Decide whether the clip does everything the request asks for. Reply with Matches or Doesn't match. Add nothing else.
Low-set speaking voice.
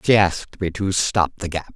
Matches